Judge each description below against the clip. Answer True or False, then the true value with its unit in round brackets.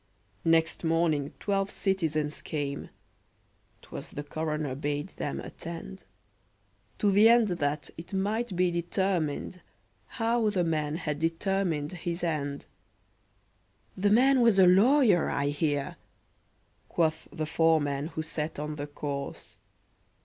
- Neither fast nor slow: False (120 wpm)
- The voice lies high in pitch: False (165 Hz)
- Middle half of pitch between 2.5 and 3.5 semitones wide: False (4.5 semitones)